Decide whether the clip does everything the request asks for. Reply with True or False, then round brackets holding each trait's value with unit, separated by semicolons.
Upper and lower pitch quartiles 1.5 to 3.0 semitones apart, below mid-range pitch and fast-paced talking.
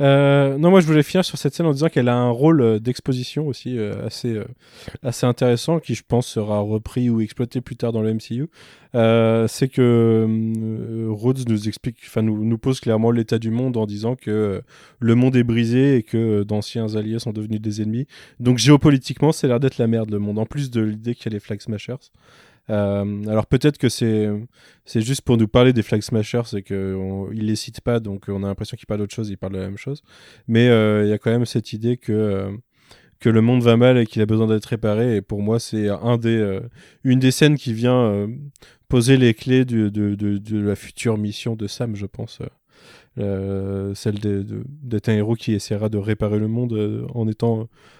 True (2.7 semitones; 115 Hz; 230 wpm)